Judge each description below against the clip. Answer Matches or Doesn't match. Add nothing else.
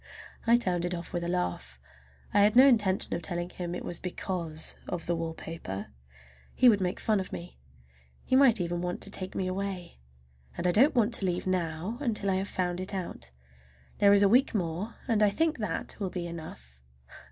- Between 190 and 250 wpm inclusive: Matches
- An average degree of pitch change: Matches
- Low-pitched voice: Doesn't match